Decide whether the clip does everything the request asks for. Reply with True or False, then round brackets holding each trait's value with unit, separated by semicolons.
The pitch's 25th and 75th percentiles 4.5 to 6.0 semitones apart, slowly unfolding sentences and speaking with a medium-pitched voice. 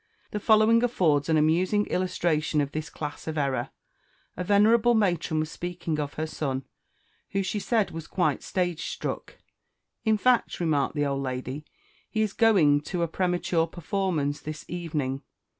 False (4.8 semitones; 160 wpm; 170 Hz)